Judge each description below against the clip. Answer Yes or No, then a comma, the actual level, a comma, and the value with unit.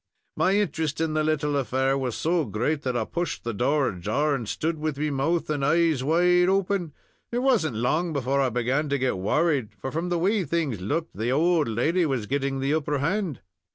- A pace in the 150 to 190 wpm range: No, fast, 205 wpm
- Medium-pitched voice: Yes, medium, 150 Hz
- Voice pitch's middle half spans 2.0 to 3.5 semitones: No, average, 4.1 semitones